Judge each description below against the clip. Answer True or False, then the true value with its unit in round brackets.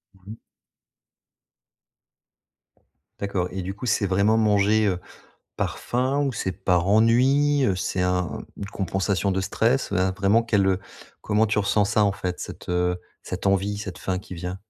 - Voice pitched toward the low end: True (100 Hz)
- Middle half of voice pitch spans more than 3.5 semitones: False (2.8 semitones)